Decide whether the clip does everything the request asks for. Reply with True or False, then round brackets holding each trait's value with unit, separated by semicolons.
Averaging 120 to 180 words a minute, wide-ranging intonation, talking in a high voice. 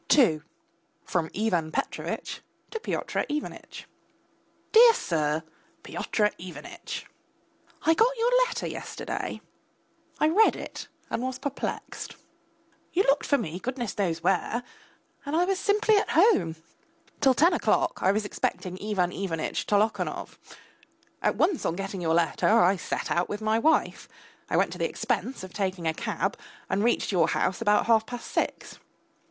True (150 wpm; 8.7 semitones; 215 Hz)